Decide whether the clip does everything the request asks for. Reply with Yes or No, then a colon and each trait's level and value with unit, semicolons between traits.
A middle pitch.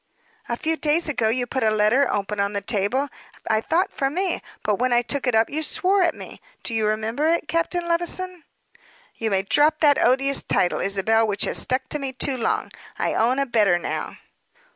No: very high, 255 Hz